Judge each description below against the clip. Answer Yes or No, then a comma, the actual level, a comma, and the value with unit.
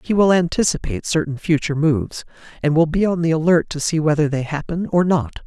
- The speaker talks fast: Yes, fast, 210 wpm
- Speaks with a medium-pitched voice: Yes, medium, 160 Hz